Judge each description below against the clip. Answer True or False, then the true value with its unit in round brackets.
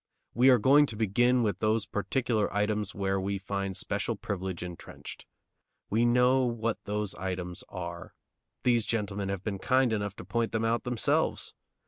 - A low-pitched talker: True (105 Hz)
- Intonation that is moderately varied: True (3.3 semitones)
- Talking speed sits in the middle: True (160 wpm)